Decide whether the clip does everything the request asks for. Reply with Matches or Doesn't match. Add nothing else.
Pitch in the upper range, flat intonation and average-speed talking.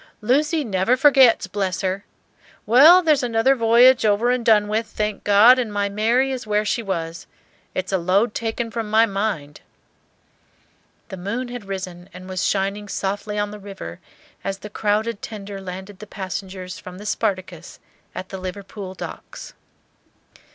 Doesn't match